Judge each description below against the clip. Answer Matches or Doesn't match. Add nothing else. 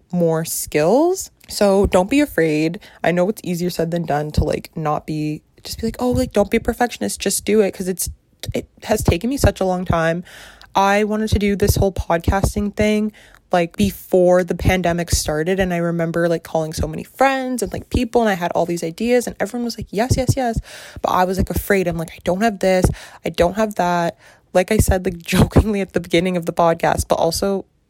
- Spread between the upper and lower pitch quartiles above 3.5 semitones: Matches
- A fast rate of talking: Matches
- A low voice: Doesn't match